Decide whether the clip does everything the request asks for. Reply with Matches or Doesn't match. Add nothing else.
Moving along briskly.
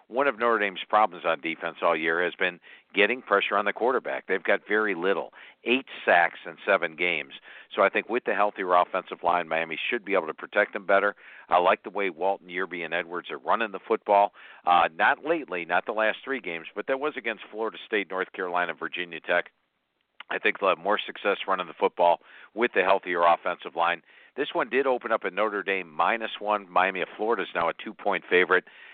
Matches